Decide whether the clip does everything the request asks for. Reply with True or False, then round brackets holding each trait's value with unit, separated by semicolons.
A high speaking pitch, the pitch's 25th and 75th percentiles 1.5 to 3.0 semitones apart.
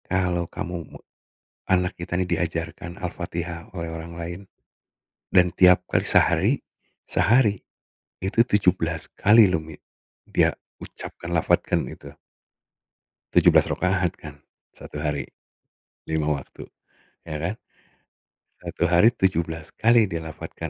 False (85 Hz; 2.4 semitones)